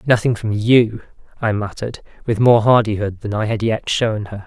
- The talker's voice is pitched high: No, low, 110 Hz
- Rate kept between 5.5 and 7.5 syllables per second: No, 5.1 syllables/s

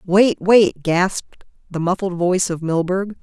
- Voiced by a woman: Yes, female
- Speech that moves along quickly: No, average, 150 wpm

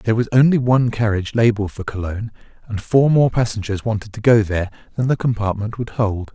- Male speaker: Yes, male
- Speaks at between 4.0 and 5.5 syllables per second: No, 6.4 syllables/s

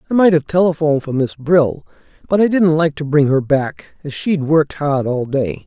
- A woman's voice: No, male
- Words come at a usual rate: No, fast, 220 wpm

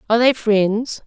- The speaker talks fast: No, average, 170 wpm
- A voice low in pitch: No, high, 225 Hz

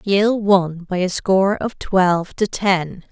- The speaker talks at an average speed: Yes, average, 175 wpm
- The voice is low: No, high, 190 Hz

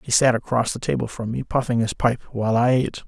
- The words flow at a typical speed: No, fast, 255 wpm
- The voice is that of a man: Yes, male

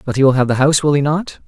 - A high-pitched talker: No, medium, 140 Hz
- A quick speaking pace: Yes, fast, 365 wpm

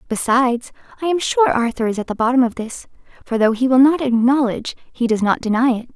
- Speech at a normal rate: No, fast, 220 wpm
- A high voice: Yes, very high, 250 Hz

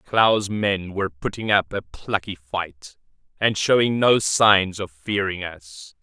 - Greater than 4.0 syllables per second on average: No, 3.6 syllables/s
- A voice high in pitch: No, very low, 95 Hz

